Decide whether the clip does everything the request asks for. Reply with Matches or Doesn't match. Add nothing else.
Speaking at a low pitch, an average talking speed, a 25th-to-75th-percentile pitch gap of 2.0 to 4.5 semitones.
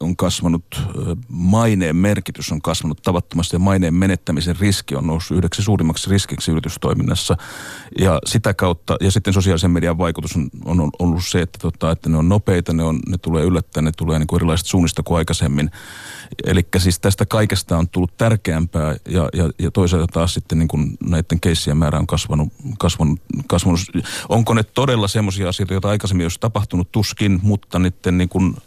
Doesn't match